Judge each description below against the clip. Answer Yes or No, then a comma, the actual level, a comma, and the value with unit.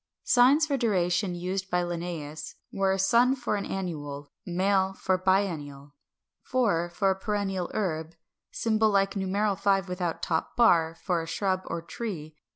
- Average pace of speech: Yes, average, 160 wpm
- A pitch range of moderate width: Yes, average, 3.1 semitones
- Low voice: No, high, 190 Hz